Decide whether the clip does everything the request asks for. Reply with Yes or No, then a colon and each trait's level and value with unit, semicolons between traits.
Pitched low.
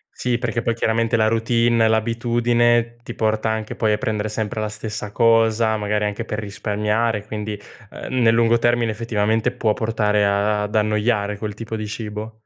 Yes: low, 110 Hz